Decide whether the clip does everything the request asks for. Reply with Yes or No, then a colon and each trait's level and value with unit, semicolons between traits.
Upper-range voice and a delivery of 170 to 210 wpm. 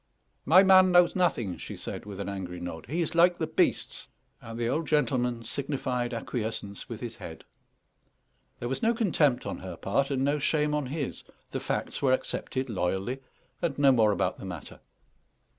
No: low, 130 Hz; average, 180 wpm